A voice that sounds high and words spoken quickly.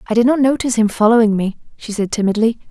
Yes: high, 225 Hz; fast, 220 wpm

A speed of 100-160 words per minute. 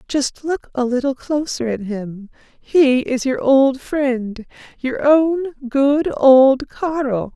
Yes: average, 140 wpm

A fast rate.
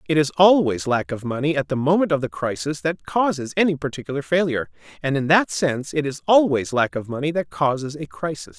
Yes: fast, 215 wpm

